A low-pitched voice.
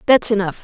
No: high, 215 Hz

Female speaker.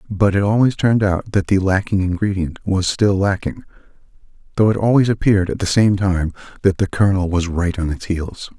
No: male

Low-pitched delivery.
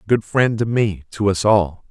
Yes: low, 100 Hz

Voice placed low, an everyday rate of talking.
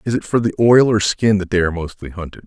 No: low, 100 Hz; fast, 290 wpm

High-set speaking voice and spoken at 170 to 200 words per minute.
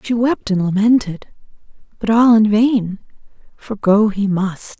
No: high, 210 Hz; average, 150 wpm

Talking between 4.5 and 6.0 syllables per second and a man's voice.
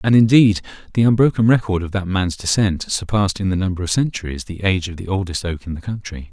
No: 6.3 syllables/s; male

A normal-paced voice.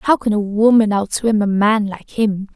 No: fast, 210 wpm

